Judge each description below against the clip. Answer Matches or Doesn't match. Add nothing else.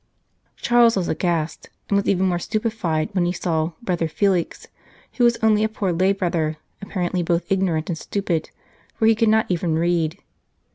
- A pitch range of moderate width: Matches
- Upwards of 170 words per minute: Matches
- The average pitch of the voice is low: Doesn't match